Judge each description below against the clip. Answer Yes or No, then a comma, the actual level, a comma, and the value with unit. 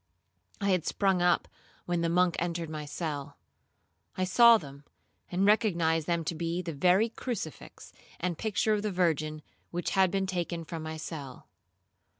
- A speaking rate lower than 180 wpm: Yes, average, 160 wpm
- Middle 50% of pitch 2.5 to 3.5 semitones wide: Yes, average, 3.0 semitones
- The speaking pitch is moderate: Yes, medium, 175 Hz